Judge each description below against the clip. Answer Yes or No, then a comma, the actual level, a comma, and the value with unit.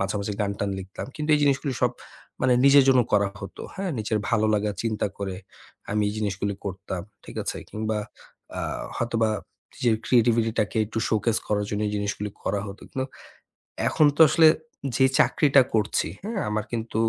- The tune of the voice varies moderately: Yes, average, 3.8 semitones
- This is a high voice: No, low, 110 Hz